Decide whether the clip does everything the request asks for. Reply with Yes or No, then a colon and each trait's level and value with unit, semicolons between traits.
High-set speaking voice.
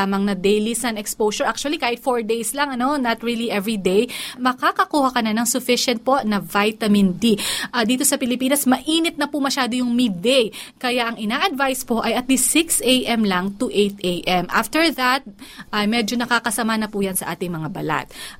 Yes: high, 240 Hz